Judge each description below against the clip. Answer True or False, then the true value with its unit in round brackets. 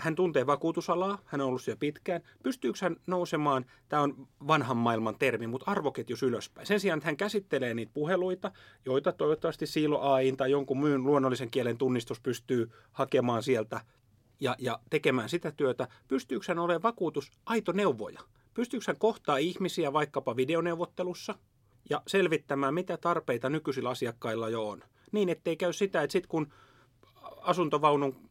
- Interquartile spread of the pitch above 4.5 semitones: True (5.3 semitones)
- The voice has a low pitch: False (150 Hz)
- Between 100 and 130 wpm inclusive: False (155 wpm)